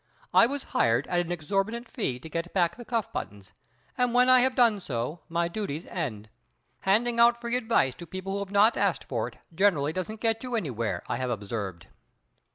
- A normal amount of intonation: No, wide, 8.5 semitones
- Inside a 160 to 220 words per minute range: Yes, average, 200 wpm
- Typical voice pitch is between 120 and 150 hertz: No, high, 190 Hz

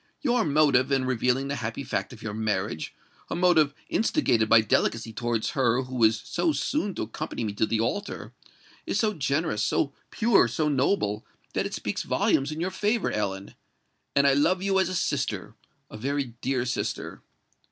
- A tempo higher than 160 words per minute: Yes, average, 170 wpm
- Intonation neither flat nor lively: No, wide, 6.8 semitones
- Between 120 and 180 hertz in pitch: Yes, low, 135 Hz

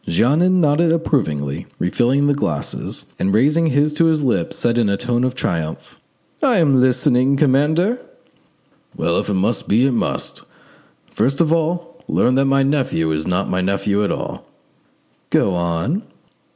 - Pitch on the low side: Yes, low, 130 Hz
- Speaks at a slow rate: No, average, 160 wpm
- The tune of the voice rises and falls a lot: Yes, wide, 7.5 semitones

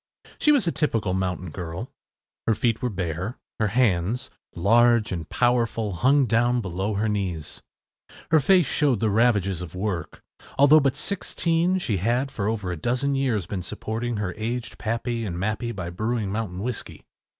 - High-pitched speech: No, low, 110 Hz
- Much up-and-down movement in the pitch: No, average, 4.5 semitones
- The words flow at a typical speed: Yes, average, 165 wpm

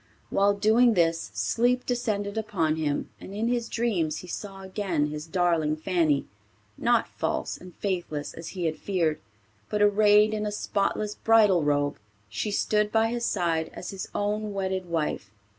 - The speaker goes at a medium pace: Yes, average, 160 wpm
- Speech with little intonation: No, average, 4.5 semitones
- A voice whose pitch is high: Yes, high, 195 Hz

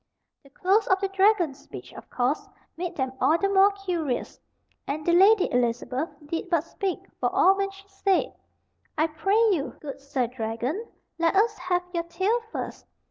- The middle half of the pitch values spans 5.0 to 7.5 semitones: Yes, wide, 5.6 semitones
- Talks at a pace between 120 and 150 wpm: No, average, 175 wpm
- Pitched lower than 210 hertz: No, very high, 345 Hz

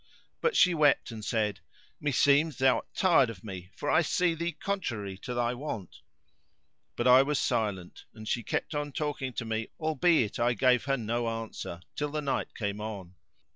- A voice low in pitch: Yes, low, 125 Hz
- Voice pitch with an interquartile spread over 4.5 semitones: Yes, average, 5.3 semitones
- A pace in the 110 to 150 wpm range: No, average, 180 wpm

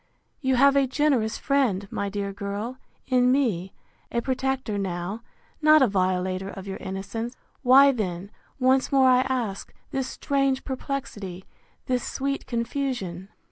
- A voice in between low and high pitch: No, high, 245 Hz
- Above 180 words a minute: No, average, 140 wpm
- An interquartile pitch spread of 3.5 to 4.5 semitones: No, average, 5.2 semitones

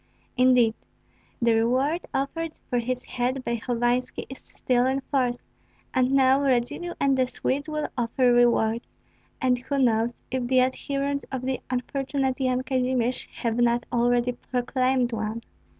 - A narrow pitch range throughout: Yes, narrow, 1.7 semitones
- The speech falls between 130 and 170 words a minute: Yes, average, 145 wpm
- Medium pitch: No, very high, 255 Hz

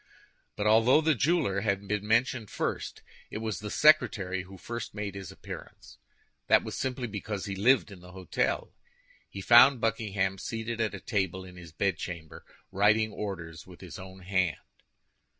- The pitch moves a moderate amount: Yes, average, 3.2 semitones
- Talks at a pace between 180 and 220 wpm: No, average, 165 wpm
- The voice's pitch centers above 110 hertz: No, low, 100 Hz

